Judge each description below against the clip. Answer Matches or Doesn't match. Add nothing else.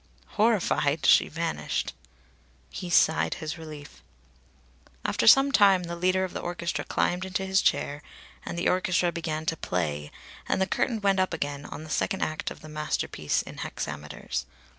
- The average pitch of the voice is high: Doesn't match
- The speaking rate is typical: Matches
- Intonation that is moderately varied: Matches